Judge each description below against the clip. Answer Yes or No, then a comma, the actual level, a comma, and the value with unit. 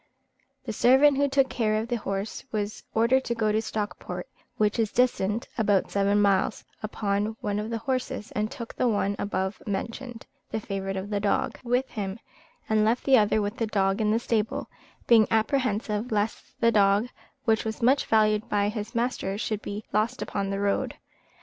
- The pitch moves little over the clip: Yes, narrow, 2.3 semitones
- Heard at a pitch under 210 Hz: No, high, 215 Hz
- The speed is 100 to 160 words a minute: No, average, 185 wpm